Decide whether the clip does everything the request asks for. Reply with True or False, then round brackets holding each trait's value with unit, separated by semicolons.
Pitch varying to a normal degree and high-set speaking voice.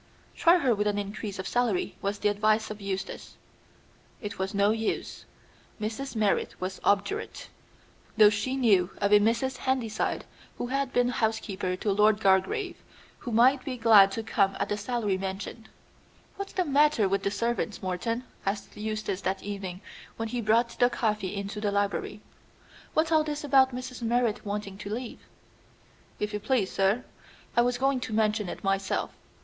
True (3.5 semitones; 215 Hz)